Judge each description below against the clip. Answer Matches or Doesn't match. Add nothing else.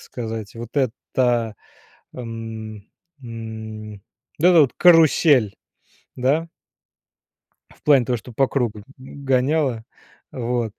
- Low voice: Matches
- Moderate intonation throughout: Matches